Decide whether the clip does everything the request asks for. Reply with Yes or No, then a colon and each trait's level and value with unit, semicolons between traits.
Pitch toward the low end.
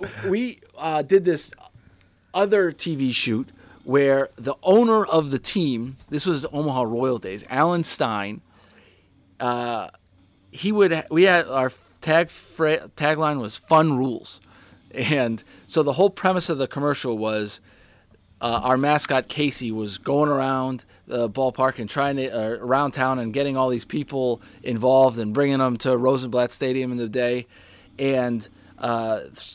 Yes: low, 130 Hz